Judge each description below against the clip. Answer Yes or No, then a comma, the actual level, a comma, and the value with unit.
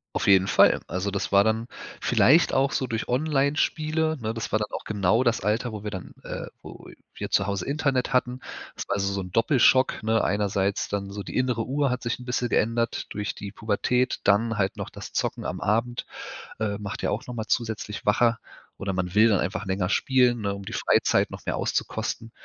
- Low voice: Yes, low, 110 Hz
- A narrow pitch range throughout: No, average, 3.7 semitones